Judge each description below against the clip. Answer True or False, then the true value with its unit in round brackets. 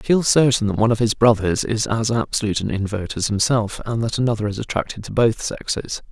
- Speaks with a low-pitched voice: True (110 Hz)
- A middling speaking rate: False (225 wpm)